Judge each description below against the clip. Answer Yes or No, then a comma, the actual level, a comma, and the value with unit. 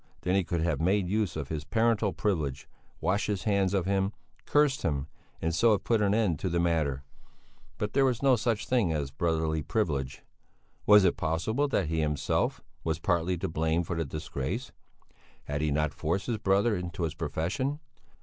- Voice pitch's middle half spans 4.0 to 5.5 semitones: Yes, average, 4.8 semitones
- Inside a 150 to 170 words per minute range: No, average, 190 wpm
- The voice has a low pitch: Yes, very low, 90 Hz